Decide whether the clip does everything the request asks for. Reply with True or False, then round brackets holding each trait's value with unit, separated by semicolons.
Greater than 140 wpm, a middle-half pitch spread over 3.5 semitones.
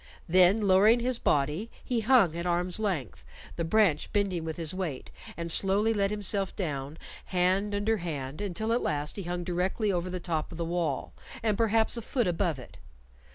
True (185 wpm; 3.9 semitones)